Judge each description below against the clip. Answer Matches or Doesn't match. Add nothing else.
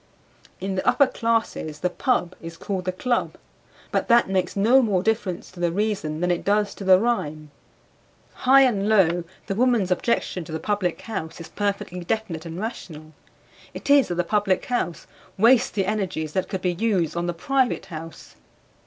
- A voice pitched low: Doesn't match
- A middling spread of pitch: Matches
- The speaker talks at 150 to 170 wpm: Doesn't match